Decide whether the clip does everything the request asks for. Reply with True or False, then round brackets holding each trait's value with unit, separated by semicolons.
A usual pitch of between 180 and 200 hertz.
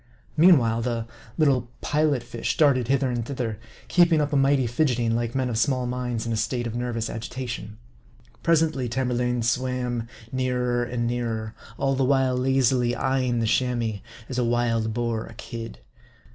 False (125 Hz)